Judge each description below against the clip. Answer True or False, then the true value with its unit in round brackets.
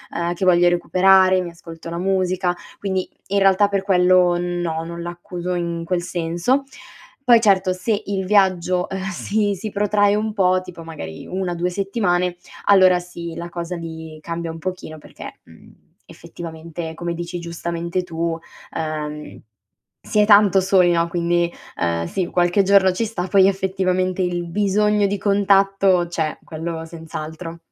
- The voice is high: False (180 Hz)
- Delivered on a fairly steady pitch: True (2.2 semitones)